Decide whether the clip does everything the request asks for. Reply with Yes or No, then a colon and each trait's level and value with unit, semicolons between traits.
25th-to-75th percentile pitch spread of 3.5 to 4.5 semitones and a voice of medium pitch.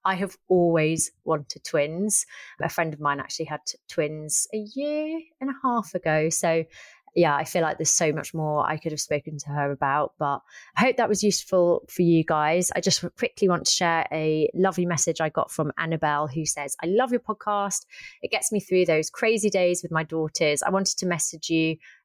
Yes: average, 4.0 semitones; medium, 165 Hz